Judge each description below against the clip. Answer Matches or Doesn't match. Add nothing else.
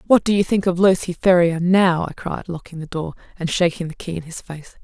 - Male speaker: Doesn't match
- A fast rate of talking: Matches